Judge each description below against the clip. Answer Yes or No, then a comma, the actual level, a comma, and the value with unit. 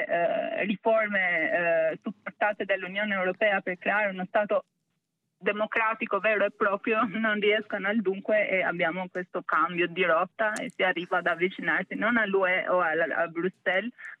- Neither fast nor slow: Yes, average, 150 wpm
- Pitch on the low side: No, high, 200 Hz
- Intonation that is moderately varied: Yes, average, 3.1 semitones